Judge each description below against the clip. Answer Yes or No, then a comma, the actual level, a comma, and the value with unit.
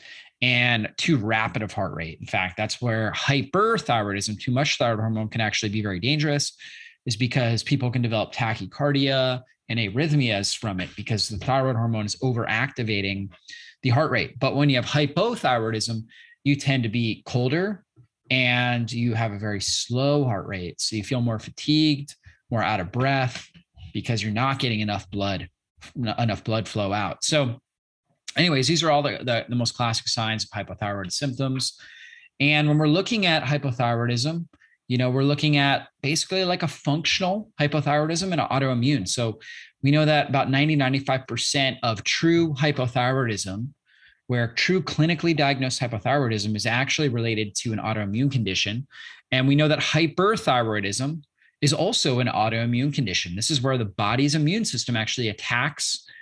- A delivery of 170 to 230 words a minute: No, average, 160 wpm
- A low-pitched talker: Yes, low, 125 Hz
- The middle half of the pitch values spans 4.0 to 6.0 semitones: Yes, average, 4.9 semitones